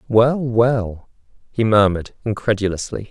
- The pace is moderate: No, slow, 95 wpm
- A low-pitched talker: Yes, low, 110 Hz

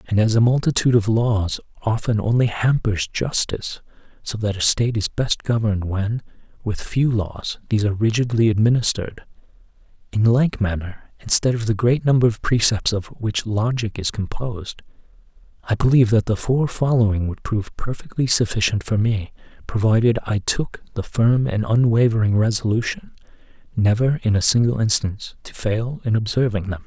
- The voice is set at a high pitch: No, low, 110 Hz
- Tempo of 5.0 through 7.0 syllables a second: Yes, 5.3 syllables/s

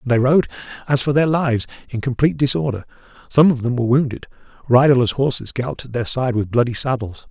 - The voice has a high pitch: No, low, 125 Hz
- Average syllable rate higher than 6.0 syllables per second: Yes, 6.5 syllables/s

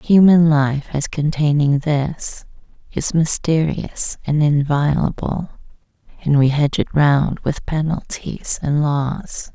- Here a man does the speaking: No, female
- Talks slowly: Yes, slow, 115 wpm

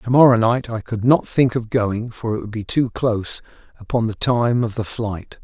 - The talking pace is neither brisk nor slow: No, fast, 230 wpm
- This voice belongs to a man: Yes, male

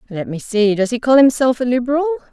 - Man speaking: No, female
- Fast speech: Yes, fast, 235 wpm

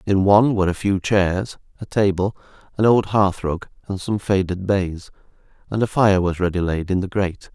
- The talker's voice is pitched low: Yes, very low, 95 Hz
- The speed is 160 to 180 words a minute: No, average, 200 wpm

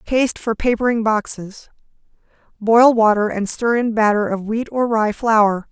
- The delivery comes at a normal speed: Yes, average, 145 wpm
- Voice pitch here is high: Yes, high, 220 Hz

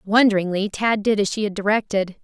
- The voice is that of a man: No, female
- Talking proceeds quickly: No, average, 190 wpm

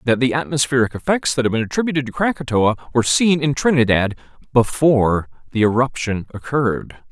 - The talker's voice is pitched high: No, low, 130 Hz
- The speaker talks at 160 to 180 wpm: No, average, 150 wpm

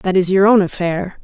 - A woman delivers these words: Yes, female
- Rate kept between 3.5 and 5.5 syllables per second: Yes, 5.0 syllables/s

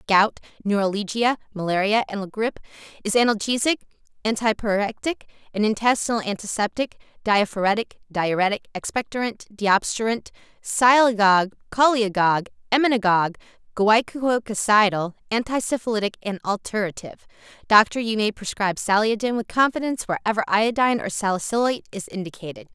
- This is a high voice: Yes, high, 215 Hz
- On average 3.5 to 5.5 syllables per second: No, 5.9 syllables/s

